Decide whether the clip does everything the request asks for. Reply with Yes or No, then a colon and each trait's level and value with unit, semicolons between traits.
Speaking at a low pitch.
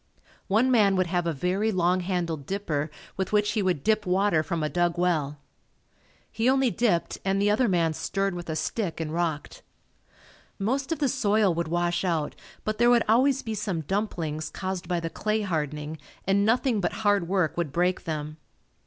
No: medium, 185 Hz